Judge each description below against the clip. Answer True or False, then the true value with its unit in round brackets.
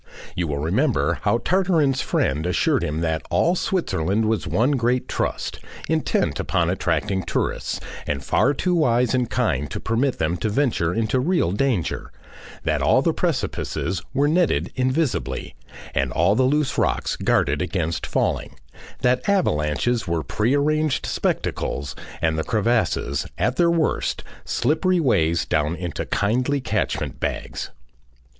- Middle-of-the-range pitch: False (115 Hz)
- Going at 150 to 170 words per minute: False (140 wpm)